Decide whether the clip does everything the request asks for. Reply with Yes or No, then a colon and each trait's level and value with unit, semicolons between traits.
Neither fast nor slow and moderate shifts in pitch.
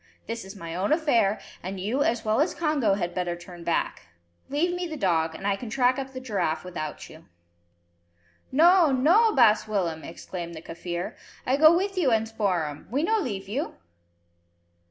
No: average, 180 wpm; wide, 8.1 semitones